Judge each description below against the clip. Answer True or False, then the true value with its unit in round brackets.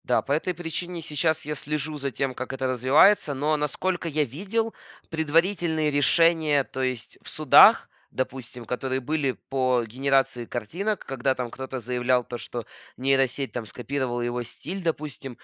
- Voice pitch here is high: False (135 Hz)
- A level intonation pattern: False (3.7 semitones)